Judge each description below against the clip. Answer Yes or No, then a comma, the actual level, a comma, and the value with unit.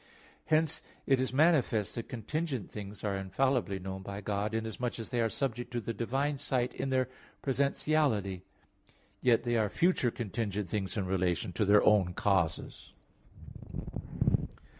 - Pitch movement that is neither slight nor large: Yes, average, 4.6 semitones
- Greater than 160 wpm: No, average, 145 wpm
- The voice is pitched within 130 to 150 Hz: No, low, 115 Hz